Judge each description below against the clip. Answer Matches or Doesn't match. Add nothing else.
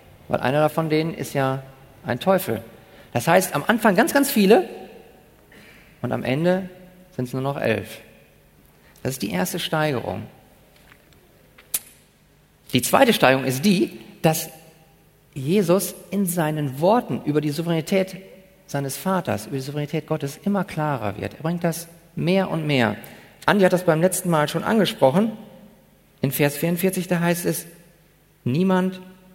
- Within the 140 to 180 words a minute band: Matches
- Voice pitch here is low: Doesn't match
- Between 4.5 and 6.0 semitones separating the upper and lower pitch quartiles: Matches